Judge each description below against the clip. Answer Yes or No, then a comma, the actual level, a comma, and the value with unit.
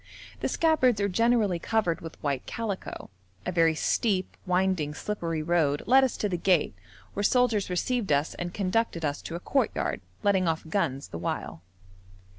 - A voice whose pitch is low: No, medium, 185 Hz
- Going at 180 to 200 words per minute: No, average, 165 wpm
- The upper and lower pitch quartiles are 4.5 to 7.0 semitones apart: Yes, average, 4.8 semitones